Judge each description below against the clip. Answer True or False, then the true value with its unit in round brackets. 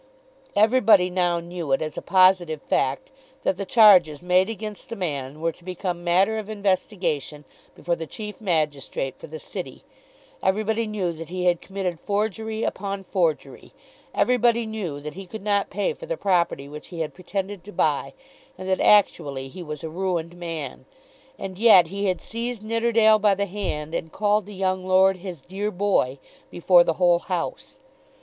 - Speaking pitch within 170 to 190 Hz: True (185 Hz)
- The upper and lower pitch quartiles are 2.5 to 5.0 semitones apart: True (3.7 semitones)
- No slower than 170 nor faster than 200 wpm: True (175 wpm)